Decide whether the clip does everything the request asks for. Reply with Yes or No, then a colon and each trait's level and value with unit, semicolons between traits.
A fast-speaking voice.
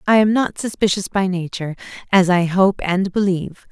No: average, 180 wpm